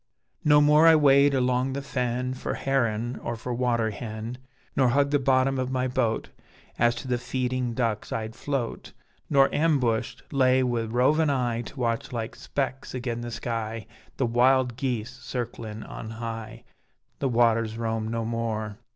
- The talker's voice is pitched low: Yes, low, 125 Hz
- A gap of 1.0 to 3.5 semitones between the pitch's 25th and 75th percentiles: Yes, narrow, 2.4 semitones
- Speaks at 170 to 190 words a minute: No, average, 160 wpm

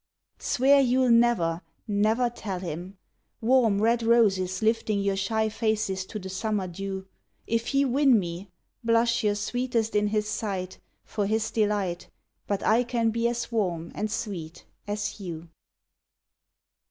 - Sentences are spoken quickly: No, average, 145 wpm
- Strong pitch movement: No, average, 3.2 semitones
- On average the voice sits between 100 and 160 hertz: No, high, 215 Hz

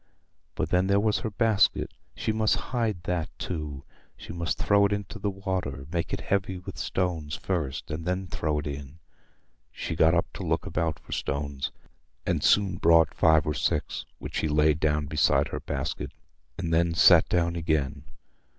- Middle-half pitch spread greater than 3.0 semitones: Yes, average, 3.8 semitones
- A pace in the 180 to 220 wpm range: No, average, 170 wpm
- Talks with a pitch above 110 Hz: No, very low, 85 Hz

